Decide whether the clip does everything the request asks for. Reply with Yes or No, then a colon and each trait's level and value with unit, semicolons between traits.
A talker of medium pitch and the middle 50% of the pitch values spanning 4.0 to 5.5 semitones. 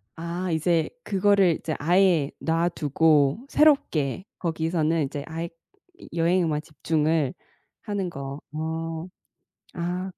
No: medium, 165 Hz; narrow, 2.6 semitones